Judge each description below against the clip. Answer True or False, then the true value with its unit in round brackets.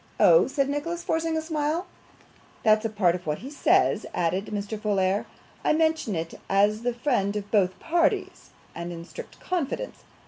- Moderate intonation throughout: False (8.3 semitones)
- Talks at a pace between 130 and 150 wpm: False (170 wpm)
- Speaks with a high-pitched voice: True (225 Hz)